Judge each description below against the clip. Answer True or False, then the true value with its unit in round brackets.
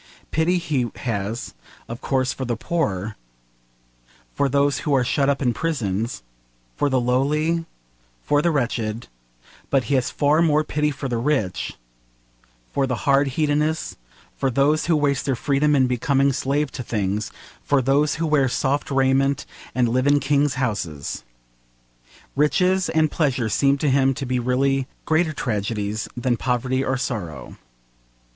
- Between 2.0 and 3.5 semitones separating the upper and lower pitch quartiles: True (3.1 semitones)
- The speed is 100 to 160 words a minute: True (150 wpm)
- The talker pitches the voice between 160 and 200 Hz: False (135 Hz)